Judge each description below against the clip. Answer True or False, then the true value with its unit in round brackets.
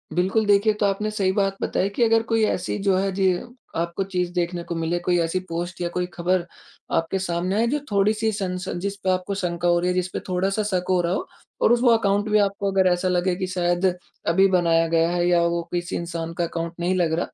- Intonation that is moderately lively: False (2.3 semitones)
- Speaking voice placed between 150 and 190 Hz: True (185 Hz)